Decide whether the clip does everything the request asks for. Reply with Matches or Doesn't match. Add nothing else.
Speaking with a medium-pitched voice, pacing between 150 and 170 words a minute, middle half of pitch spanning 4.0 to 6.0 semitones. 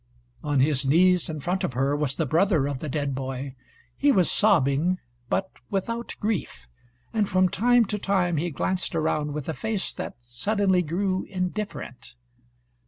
Matches